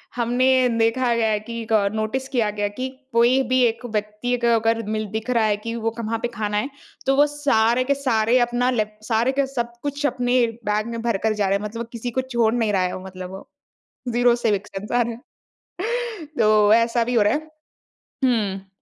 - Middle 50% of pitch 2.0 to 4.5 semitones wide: Yes, average, 2.7 semitones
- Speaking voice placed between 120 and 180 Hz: No, high, 230 Hz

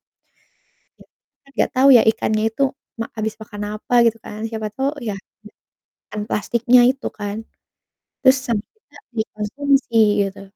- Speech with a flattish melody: No, average, 3.3 semitones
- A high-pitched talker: Yes, high, 220 Hz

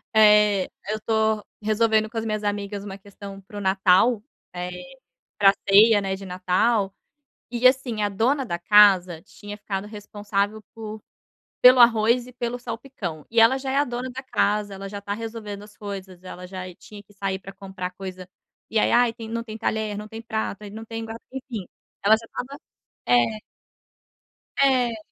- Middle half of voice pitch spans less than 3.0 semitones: Yes, narrow, 2.5 semitones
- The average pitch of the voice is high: Yes, high, 210 Hz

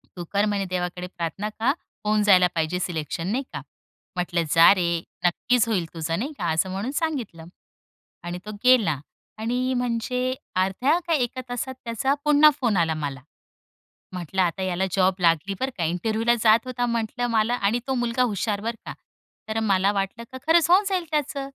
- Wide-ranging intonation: Yes, wide, 5.7 semitones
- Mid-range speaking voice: No, high, 215 Hz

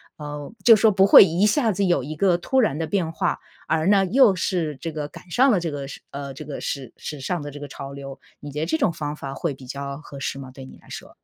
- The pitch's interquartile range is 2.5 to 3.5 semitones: No, average, 5.0 semitones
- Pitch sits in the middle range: Yes, medium, 155 Hz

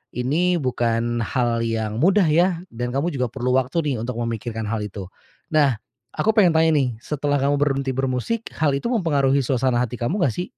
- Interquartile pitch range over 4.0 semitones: Yes, average, 4.6 semitones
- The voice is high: No, low, 135 Hz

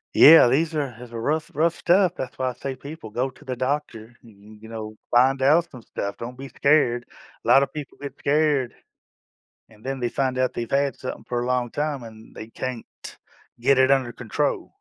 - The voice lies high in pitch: No, low, 130 Hz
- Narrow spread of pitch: No, average, 3.1 semitones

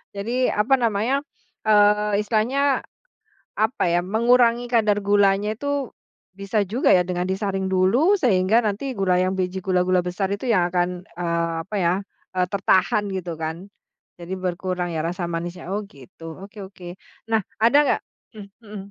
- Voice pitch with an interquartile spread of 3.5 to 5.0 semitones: No, average, 2.9 semitones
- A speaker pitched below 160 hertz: No, high, 195 Hz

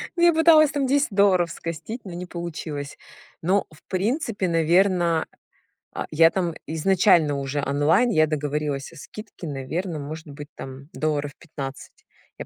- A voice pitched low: No, medium, 165 Hz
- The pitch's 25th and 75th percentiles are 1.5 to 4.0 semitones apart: No, average, 4.7 semitones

